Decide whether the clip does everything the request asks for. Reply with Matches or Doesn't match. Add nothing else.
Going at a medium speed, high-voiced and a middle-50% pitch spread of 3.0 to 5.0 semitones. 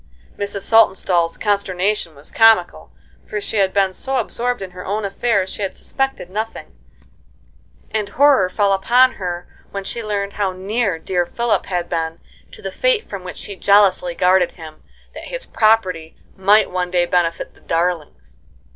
Matches